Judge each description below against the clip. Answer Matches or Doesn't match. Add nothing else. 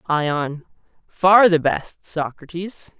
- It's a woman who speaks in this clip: Doesn't match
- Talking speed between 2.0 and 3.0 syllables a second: Matches